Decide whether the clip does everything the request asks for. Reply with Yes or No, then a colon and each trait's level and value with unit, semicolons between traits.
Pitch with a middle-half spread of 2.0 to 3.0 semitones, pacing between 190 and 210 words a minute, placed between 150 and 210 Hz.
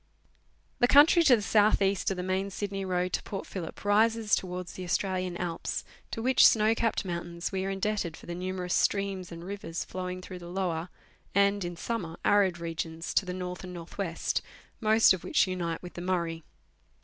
Yes: narrow, 2.5 semitones; average, 195 wpm; medium, 185 Hz